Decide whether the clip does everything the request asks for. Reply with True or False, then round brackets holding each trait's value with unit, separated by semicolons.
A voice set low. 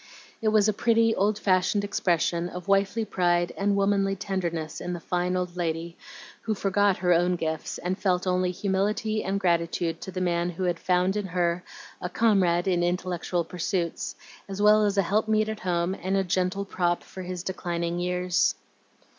False (185 Hz)